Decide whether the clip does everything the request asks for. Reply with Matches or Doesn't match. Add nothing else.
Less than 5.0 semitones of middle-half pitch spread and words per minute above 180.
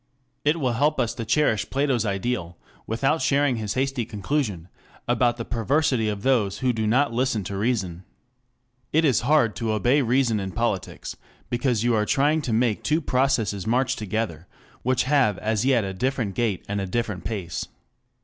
Doesn't match